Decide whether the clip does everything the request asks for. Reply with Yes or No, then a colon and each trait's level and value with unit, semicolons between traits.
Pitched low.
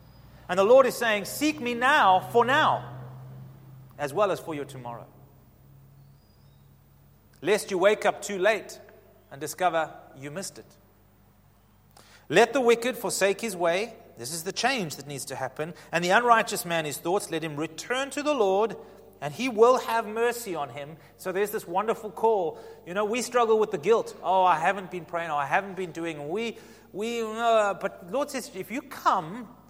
No: medium, 185 Hz